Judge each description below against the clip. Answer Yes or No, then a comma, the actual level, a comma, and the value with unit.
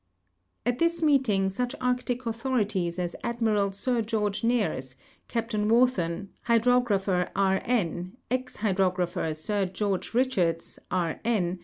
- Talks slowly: Yes, slow, 120 wpm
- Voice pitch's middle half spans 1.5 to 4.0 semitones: No, average, 4.8 semitones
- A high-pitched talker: Yes, high, 210 Hz